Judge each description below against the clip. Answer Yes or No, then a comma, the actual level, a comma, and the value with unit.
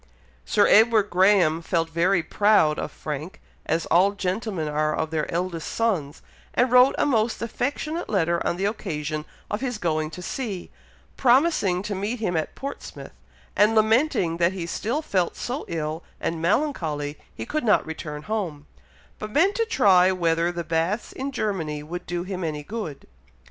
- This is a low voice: No, medium, 185 Hz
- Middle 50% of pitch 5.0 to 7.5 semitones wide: Yes, average, 5.3 semitones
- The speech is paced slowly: No, average, 165 wpm